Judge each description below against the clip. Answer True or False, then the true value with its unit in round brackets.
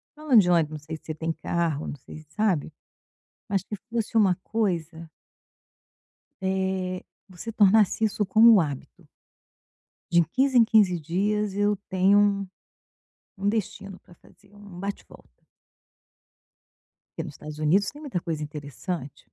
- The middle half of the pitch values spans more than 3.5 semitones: True (4.2 semitones)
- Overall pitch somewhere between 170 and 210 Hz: True (190 Hz)